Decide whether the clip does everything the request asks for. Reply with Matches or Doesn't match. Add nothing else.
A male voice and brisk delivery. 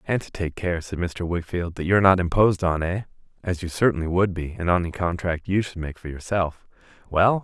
Matches